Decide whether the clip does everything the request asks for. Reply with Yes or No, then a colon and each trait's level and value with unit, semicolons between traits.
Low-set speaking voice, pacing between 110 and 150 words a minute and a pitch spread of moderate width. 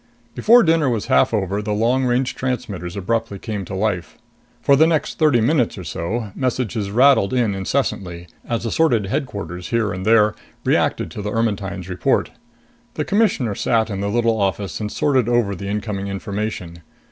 No: low, 110 Hz; average, 170 wpm; average, 4.0 semitones